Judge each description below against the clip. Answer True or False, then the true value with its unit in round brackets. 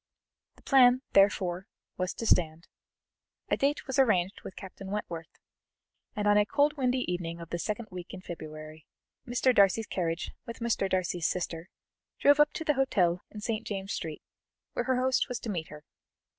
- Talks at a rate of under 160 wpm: False (175 wpm)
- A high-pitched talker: True (195 Hz)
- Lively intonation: True (6.1 semitones)